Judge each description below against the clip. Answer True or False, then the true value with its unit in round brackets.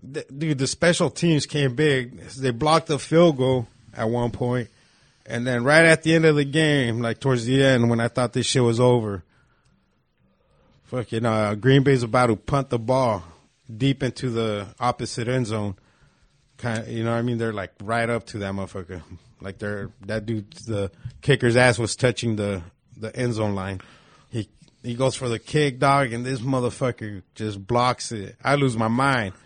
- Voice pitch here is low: True (120 Hz)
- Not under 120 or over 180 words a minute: False (195 wpm)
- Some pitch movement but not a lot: True (3.3 semitones)